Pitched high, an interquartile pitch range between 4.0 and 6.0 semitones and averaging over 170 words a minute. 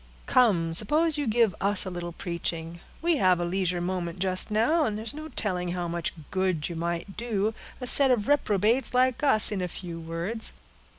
Yes: high, 195 Hz; average, 5.2 semitones; average, 190 wpm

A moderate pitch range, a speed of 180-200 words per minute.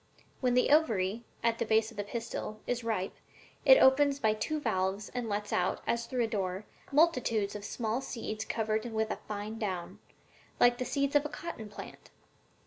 Yes: average, 3.2 semitones; average, 185 wpm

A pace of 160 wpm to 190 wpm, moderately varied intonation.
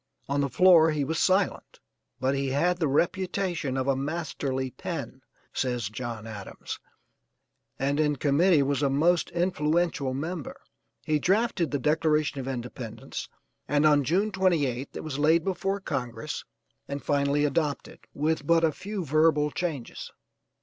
No: average, 145 wpm; average, 3.8 semitones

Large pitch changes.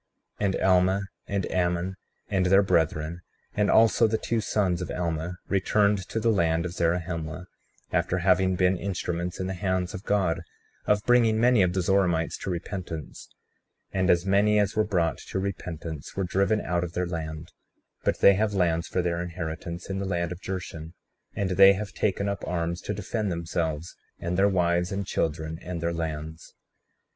No: narrow, 2.6 semitones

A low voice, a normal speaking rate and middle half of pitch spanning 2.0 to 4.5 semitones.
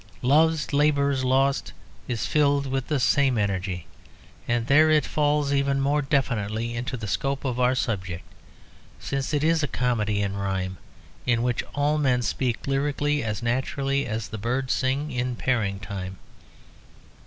Yes: low, 130 Hz; average, 155 wpm; average, 4.2 semitones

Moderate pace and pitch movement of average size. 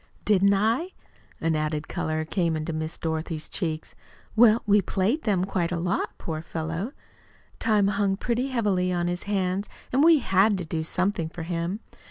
Yes: average, 170 wpm; average, 4.1 semitones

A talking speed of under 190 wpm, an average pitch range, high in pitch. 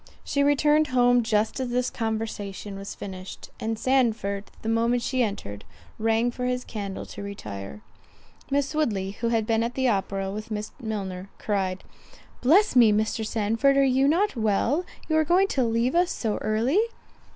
Yes: average, 170 wpm; average, 4.0 semitones; high, 225 Hz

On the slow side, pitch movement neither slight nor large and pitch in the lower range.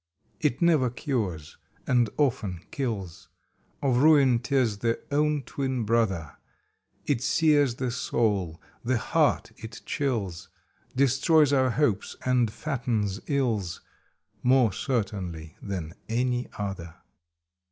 Yes: slow, 110 wpm; average, 5.0 semitones; low, 120 Hz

